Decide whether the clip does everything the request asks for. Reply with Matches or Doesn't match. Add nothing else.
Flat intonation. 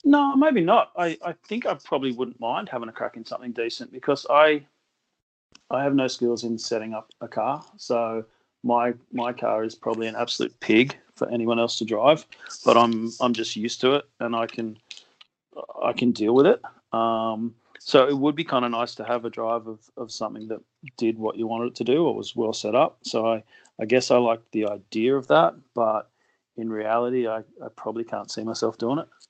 Matches